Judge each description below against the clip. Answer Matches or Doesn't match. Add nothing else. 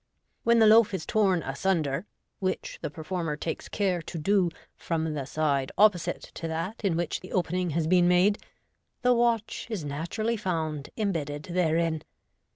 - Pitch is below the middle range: Doesn't match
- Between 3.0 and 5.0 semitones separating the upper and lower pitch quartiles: Matches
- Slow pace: Doesn't match